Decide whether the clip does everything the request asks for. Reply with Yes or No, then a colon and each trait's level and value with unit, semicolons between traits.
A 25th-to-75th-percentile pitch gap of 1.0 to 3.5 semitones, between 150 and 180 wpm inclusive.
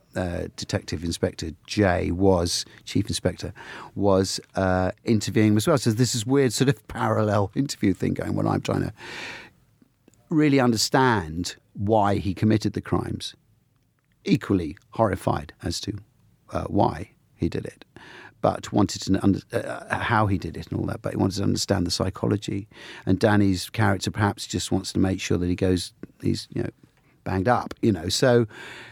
Yes: average, 3.2 semitones; average, 175 wpm